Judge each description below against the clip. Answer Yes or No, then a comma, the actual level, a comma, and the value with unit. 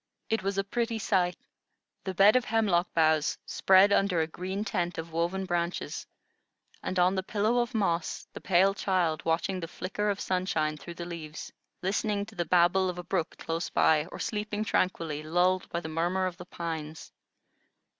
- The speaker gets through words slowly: No, average, 180 wpm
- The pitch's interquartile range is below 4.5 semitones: Yes, average, 2.8 semitones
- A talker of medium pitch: Yes, medium, 180 Hz